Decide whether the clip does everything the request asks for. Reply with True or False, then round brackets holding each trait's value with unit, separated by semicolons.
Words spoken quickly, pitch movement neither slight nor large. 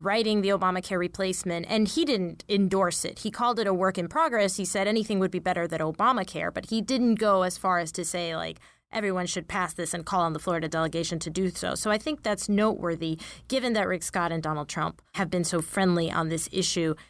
True (230 wpm; 3.3 semitones)